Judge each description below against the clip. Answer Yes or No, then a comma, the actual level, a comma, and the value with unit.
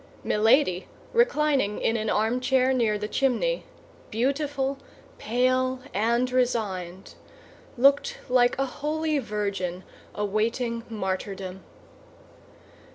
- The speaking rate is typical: No, slow, 90 wpm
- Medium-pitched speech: No, high, 240 Hz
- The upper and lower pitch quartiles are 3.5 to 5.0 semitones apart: Yes, average, 4.2 semitones